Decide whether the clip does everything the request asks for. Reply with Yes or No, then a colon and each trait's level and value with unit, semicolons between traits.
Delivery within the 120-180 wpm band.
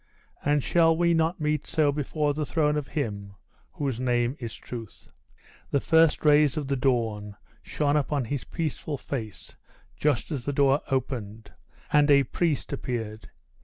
Yes: average, 155 wpm